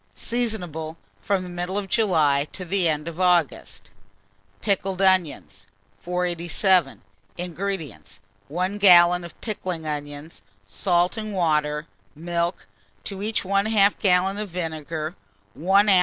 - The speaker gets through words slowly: Yes, slow, 120 wpm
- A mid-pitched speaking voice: Yes, medium, 180 Hz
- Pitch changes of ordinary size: Yes, average, 3.4 semitones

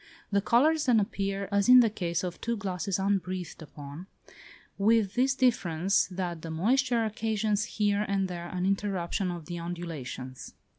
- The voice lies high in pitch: Yes, high, 195 Hz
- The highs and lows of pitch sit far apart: No, average, 3.8 semitones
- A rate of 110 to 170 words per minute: Yes, average, 155 wpm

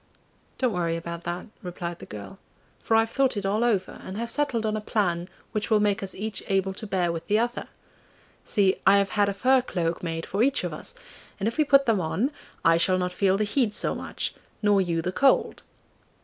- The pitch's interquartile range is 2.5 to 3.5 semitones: No, average, 4.0 semitones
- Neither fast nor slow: No, fast, 220 wpm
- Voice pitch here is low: No, high, 200 Hz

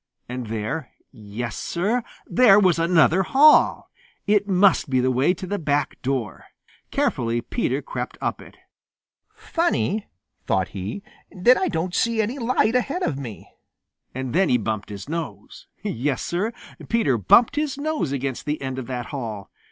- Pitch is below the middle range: No, medium, 160 Hz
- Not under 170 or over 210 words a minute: No, average, 160 wpm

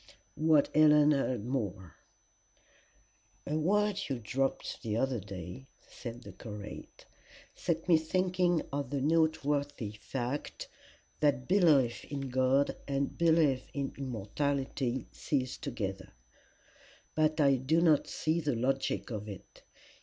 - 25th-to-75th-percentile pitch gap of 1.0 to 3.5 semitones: No, average, 4.3 semitones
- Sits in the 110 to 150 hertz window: Yes, low, 135 Hz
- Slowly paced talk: Yes, slow, 125 wpm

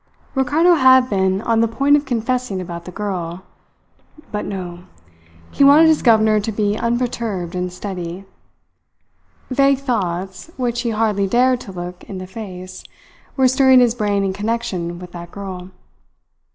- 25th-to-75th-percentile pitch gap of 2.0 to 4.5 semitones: No, average, 5.2 semitones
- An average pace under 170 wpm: Yes, average, 150 wpm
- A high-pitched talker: Yes, high, 210 Hz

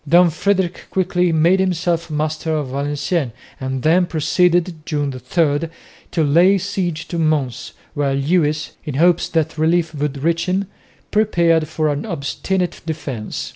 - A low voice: No, medium, 160 Hz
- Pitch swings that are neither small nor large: Yes, average, 3.2 semitones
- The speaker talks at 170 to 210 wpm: No, average, 140 wpm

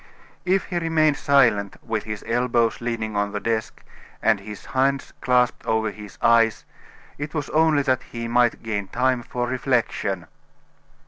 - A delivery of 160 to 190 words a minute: No, average, 150 wpm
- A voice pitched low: Yes, low, 120 Hz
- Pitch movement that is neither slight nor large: Yes, average, 3.5 semitones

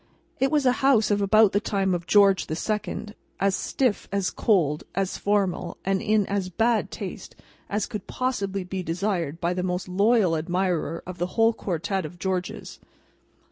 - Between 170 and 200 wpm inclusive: Yes, average, 175 wpm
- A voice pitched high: Yes, high, 195 Hz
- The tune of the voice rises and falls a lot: No, average, 2.9 semitones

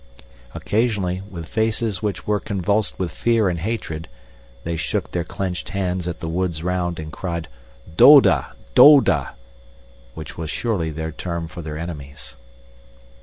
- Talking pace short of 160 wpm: Yes, average, 140 wpm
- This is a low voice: Yes, very low, 90 Hz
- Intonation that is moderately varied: Yes, average, 4.0 semitones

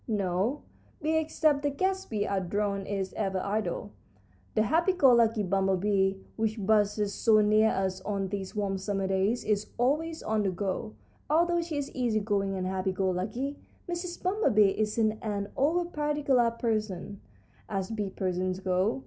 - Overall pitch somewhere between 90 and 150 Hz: No, high, 210 Hz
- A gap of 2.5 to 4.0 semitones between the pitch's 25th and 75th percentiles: No, average, 5.2 semitones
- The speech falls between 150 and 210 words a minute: Yes, average, 160 wpm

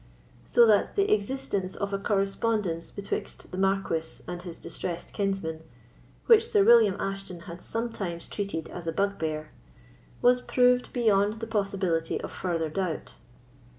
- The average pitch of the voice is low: No, high, 195 Hz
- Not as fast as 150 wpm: Yes, average, 140 wpm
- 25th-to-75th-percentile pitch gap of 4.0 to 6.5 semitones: Yes, average, 4.4 semitones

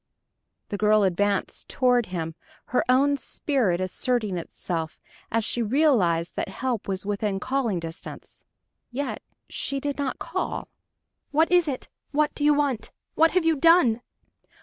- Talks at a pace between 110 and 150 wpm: Yes, average, 145 wpm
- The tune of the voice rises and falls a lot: Yes, wide, 6.5 semitones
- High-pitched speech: Yes, high, 245 Hz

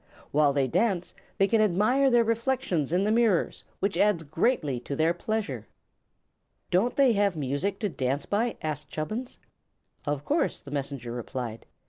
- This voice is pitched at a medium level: Yes, medium, 180 Hz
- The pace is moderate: Yes, average, 155 wpm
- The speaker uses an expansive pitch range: Yes, wide, 7.6 semitones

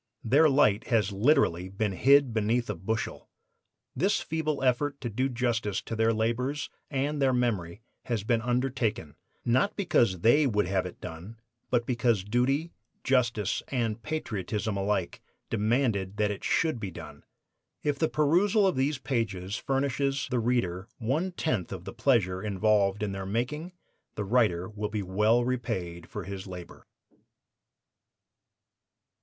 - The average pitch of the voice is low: Yes, low, 115 Hz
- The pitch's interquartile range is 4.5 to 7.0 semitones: Yes, average, 4.9 semitones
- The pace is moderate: Yes, average, 145 wpm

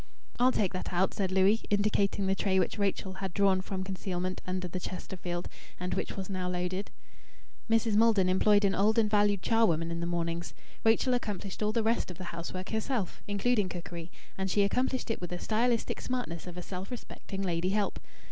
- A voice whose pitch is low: No, high, 195 Hz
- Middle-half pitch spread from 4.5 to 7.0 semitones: No, average, 2.8 semitones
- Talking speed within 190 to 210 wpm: Yes, average, 195 wpm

